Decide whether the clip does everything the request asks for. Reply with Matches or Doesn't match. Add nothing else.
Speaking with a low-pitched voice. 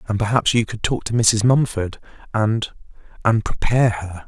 Matches